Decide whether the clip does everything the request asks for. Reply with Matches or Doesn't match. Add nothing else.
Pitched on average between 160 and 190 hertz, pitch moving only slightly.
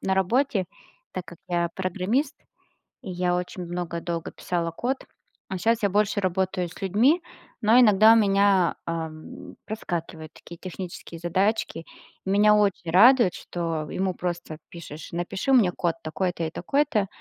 Doesn't match